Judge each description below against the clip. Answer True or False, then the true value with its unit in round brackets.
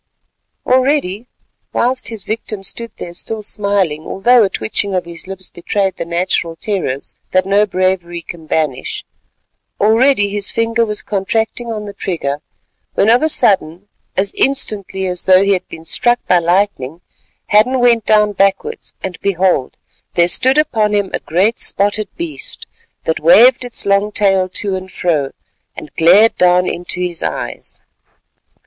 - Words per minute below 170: True (150 wpm)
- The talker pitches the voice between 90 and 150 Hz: False (195 Hz)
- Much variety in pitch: False (3.6 semitones)